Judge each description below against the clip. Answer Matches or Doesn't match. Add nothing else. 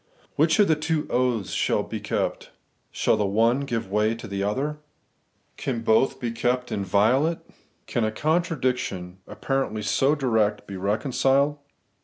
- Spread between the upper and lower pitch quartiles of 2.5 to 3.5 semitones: Doesn't match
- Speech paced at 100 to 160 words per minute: Matches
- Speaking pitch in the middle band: Doesn't match